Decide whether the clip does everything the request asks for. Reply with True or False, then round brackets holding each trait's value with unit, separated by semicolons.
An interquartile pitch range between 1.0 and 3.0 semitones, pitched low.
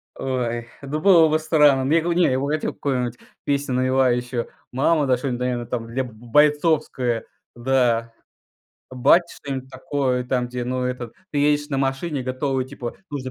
True (2.7 semitones; 130 Hz)